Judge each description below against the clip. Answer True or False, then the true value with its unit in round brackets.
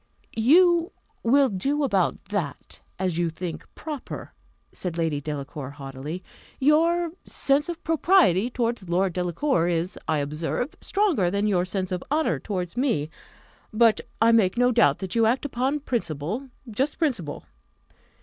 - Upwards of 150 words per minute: False (140 wpm)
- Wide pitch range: True (8.4 semitones)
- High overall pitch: True (205 Hz)